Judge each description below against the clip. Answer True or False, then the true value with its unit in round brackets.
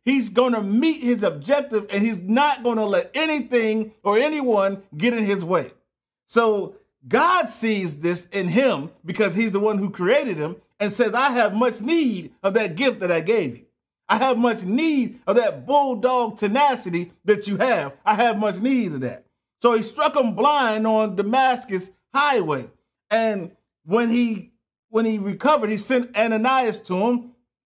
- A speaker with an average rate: True (175 wpm)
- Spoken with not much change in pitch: False (4.0 semitones)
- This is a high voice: True (225 Hz)